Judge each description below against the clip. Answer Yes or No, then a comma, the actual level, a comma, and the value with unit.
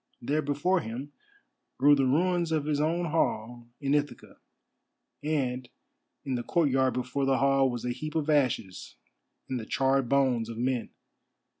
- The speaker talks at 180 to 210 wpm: No, average, 155 wpm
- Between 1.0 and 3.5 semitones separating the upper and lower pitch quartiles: Yes, average, 3.1 semitones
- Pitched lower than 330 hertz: Yes, low, 135 Hz